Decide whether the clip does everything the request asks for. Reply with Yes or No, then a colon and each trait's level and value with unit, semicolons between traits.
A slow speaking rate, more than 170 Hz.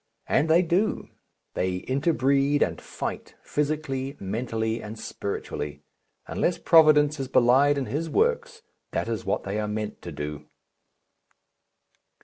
No: slow, 130 wpm; low, 135 Hz